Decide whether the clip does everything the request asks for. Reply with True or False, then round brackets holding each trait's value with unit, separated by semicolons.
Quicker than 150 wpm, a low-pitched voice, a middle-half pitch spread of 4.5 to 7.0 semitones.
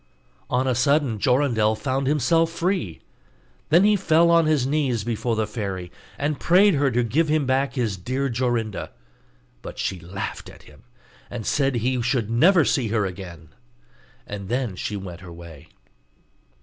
True (160 wpm; 125 Hz; 5.5 semitones)